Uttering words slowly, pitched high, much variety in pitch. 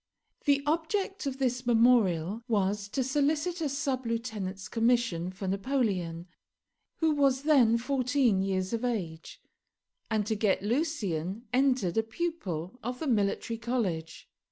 Yes: slow, 130 wpm; high, 230 Hz; wide, 5.7 semitones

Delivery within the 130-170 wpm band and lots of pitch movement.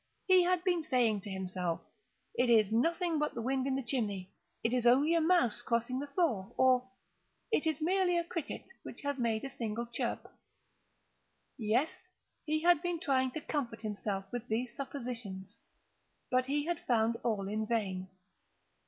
Yes: average, 160 wpm; wide, 5.8 semitones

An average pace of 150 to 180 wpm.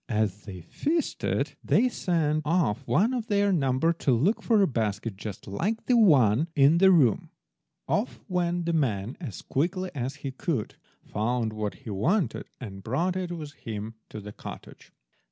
Yes: average, 170 wpm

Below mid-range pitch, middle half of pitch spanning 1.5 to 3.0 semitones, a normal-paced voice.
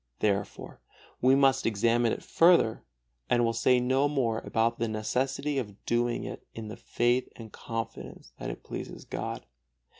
Yes: low, 120 Hz; narrow, 2.6 semitones; average, 155 wpm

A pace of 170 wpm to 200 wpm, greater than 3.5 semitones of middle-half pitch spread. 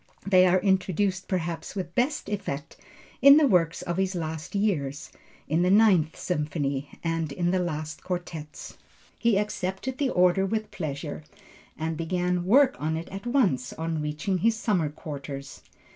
No: average, 155 wpm; average, 4.1 semitones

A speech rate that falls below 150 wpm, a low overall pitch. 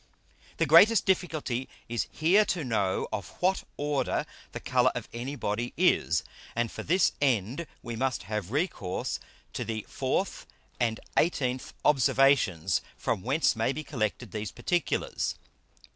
Yes: average, 140 wpm; low, 130 Hz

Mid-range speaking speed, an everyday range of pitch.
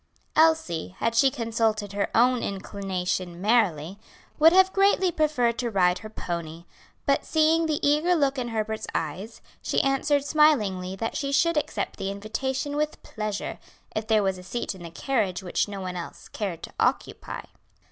No: average, 165 wpm; wide, 7.1 semitones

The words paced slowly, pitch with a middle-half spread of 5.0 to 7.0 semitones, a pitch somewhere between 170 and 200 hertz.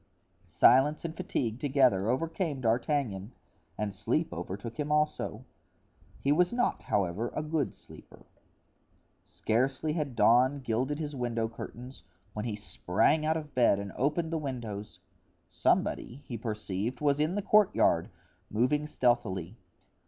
No: slow, 130 wpm; average, 5.3 semitones; low, 130 Hz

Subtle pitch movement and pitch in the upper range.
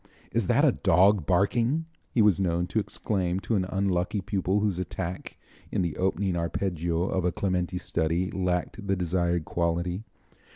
No: narrow, 2.1 semitones; very low, 90 Hz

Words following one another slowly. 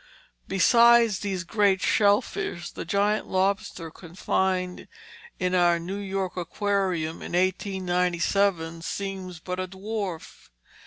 Yes: slow, 110 wpm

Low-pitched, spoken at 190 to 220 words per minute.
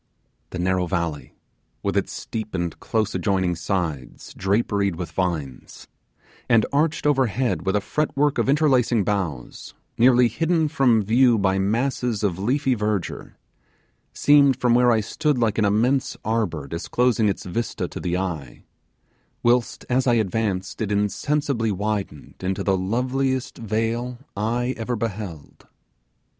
No: low, 110 Hz; average, 140 wpm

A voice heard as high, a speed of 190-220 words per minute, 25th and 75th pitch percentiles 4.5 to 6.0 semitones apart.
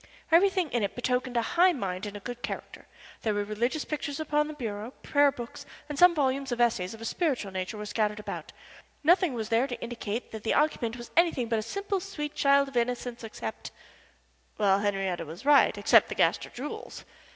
Yes: high, 240 Hz; average, 200 wpm; wide, 5.6 semitones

